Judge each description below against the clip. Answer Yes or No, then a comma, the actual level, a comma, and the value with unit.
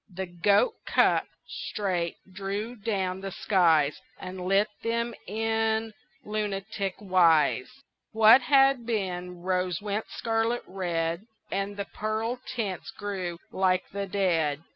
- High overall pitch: Yes, high, 195 Hz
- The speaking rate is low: Yes, slow, 120 wpm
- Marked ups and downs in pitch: No, average, 3.3 semitones